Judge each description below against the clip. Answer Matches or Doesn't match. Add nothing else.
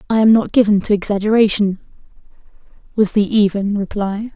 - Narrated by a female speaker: Matches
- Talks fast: Doesn't match